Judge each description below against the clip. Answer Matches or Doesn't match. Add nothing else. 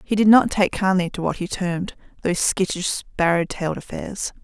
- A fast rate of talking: Doesn't match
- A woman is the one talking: Matches